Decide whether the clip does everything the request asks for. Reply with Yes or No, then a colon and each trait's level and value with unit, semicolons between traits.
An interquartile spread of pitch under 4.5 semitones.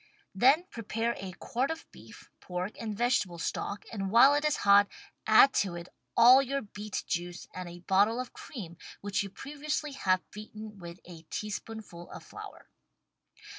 No: average, 4.8 semitones